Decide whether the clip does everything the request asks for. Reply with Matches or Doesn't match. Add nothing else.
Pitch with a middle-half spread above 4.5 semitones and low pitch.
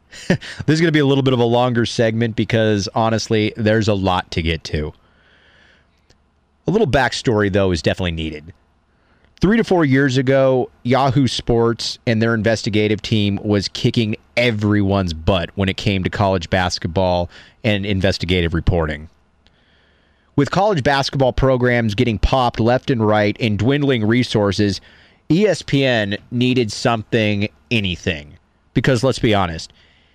Matches